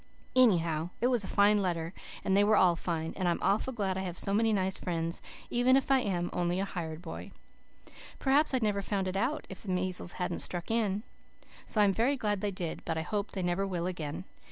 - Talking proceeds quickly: Yes, fast, 225 wpm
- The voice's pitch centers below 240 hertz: Yes, high, 190 Hz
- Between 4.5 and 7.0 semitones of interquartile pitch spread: No, average, 3.4 semitones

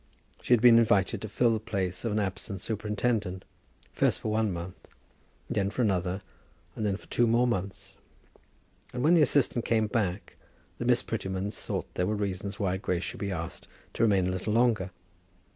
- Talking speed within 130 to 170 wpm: No, average, 185 wpm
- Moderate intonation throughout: Yes, average, 3.4 semitones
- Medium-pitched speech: No, low, 105 Hz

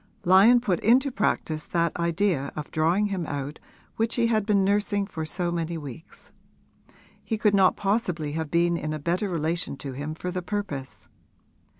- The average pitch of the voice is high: No, medium, 175 Hz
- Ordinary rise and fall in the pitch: Yes, average, 4.6 semitones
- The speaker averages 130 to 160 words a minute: No, average, 175 wpm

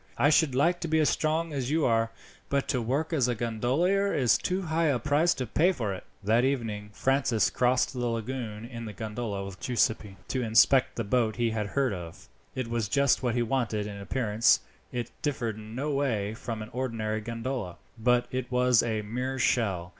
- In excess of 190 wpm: Yes, average, 200 wpm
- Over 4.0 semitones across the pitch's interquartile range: No, average, 3.7 semitones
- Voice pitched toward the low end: Yes, low, 120 Hz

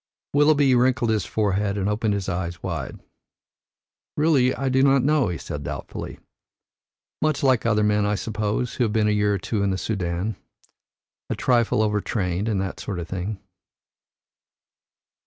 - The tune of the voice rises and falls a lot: No, average, 4.3 semitones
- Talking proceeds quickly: No, average, 160 wpm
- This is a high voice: No, low, 105 Hz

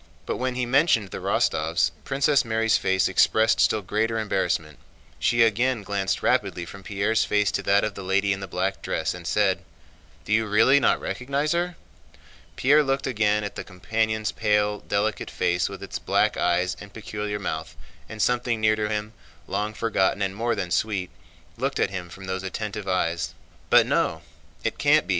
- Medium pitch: No, low, 105 Hz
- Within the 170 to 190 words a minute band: Yes, average, 180 wpm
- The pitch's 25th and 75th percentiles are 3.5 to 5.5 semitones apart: No, average, 2.7 semitones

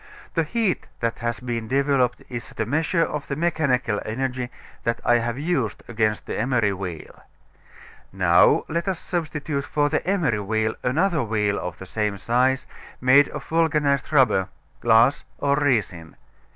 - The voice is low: Yes, low, 125 Hz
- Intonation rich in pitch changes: No, average, 5.0 semitones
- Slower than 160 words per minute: Yes, average, 150 wpm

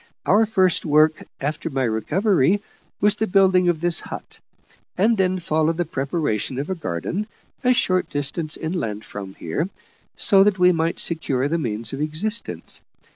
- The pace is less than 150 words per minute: No, average, 160 wpm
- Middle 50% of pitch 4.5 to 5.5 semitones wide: Yes, average, 5.1 semitones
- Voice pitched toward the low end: No, medium, 165 Hz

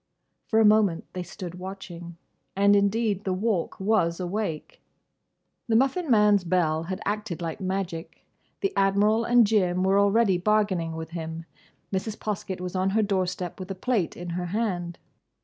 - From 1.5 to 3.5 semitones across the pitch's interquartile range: Yes, average, 3.1 semitones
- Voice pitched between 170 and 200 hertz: Yes, high, 190 Hz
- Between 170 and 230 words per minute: No, average, 160 wpm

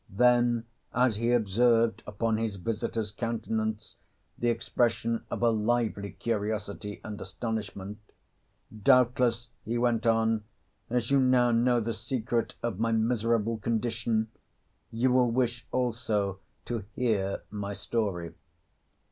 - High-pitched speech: No, low, 115 Hz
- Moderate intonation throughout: No, narrow, 2.0 semitones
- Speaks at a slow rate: Yes, slow, 120 wpm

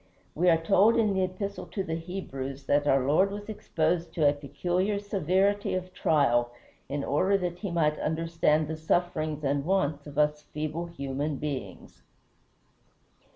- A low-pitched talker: No, medium, 165 Hz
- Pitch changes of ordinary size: Yes, average, 4.1 semitones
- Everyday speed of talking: Yes, average, 155 wpm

